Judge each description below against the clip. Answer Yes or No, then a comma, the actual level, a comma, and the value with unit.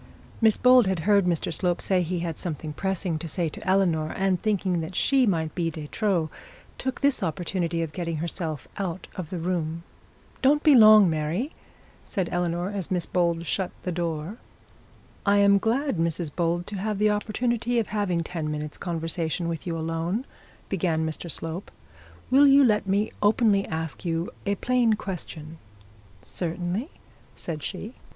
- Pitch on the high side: No, medium, 180 Hz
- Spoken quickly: No, average, 165 wpm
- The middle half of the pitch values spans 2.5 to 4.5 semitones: Yes, average, 3.9 semitones